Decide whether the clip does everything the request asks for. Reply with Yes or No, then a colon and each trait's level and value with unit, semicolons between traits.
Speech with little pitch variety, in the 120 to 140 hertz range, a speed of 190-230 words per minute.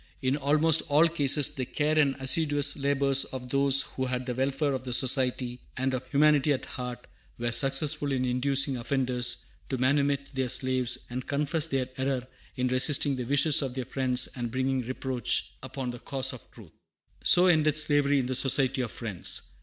No: narrow, 2.0 semitones; low, 135 Hz; average, 180 wpm